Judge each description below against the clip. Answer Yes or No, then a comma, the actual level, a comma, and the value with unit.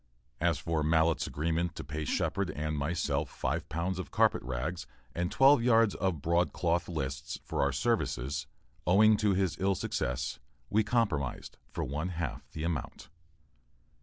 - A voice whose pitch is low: Yes, very low, 85 Hz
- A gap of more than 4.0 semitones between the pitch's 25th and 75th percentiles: Yes, average, 4.5 semitones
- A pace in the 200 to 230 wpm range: No, average, 150 wpm